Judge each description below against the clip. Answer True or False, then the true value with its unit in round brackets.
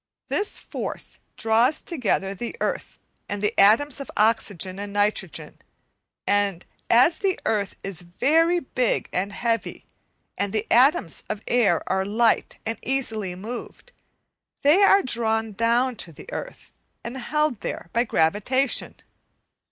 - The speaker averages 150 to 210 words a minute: False (135 wpm)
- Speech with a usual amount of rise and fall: True (4.4 semitones)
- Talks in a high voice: True (225 Hz)